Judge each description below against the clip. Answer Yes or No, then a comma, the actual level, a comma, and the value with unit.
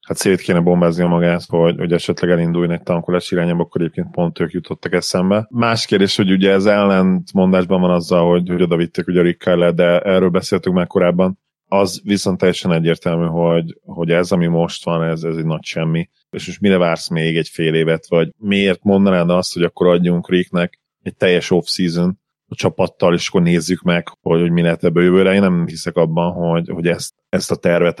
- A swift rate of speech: Yes, fast, 205 wpm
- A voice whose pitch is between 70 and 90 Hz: Yes, very low, 85 Hz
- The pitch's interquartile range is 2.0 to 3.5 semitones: No, narrow, 1.5 semitones